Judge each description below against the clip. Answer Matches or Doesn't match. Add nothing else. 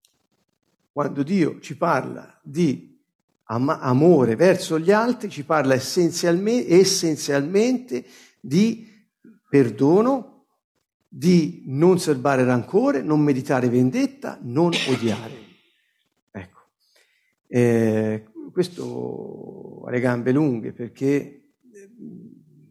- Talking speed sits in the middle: Doesn't match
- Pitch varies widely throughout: Matches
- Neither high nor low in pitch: Matches